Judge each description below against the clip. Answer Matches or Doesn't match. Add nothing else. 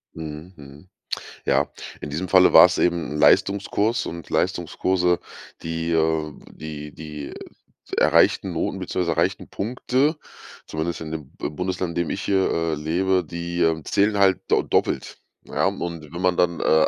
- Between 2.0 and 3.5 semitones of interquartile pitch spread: Matches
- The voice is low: Matches